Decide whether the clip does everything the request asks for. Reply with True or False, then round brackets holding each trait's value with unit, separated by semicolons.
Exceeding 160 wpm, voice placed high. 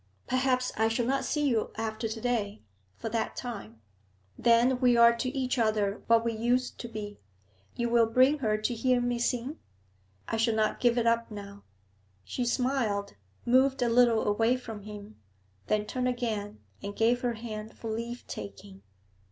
True (175 wpm; 230 Hz)